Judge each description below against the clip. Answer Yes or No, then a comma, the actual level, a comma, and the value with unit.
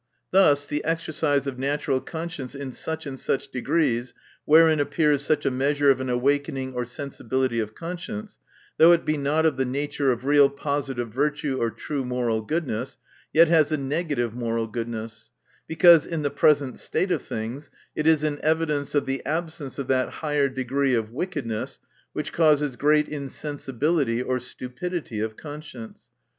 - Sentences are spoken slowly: No, average, 165 wpm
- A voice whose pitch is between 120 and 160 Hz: Yes, medium, 140 Hz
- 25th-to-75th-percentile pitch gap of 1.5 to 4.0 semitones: Yes, average, 3.3 semitones